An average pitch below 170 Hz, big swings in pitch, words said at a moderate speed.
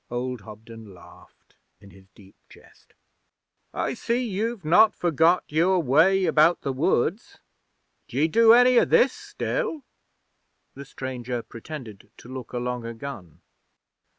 No: medium, 140 Hz; wide, 8.2 semitones; slow, 130 wpm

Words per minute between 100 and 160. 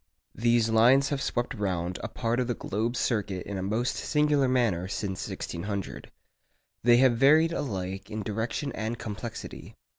Yes: average, 155 wpm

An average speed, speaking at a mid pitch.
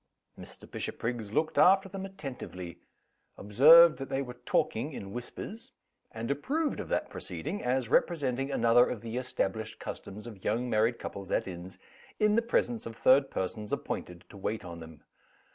No: average, 160 wpm; low, 120 Hz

